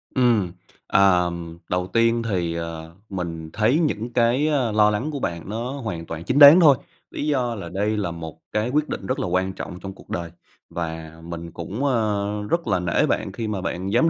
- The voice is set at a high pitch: No, low, 100 Hz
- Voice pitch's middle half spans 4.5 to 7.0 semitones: Yes, wide, 5.6 semitones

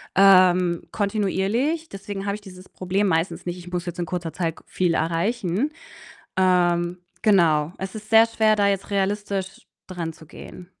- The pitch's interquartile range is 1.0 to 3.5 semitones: Yes, narrow, 2.6 semitones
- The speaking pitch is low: No, high, 190 Hz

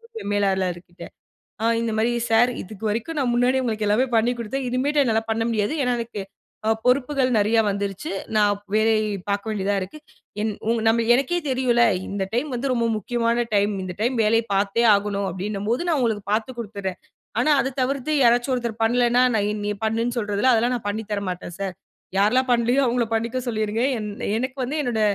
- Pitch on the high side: Yes, high, 225 Hz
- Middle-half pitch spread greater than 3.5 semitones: No, average, 3.1 semitones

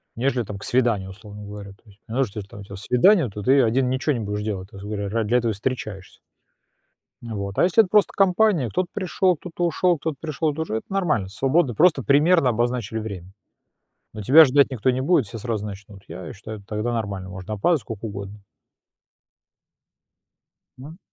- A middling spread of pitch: No, wide, 6.1 semitones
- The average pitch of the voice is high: No, low, 115 Hz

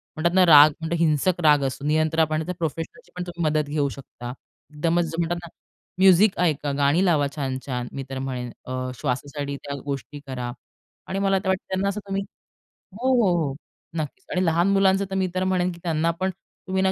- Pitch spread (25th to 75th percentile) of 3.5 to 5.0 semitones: Yes, average, 4.5 semitones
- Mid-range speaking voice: Yes, medium, 160 Hz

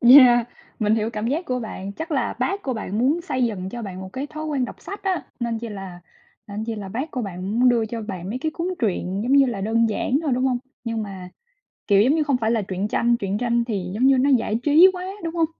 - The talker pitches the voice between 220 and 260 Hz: Yes, high, 235 Hz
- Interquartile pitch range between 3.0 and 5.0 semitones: Yes, average, 4.6 semitones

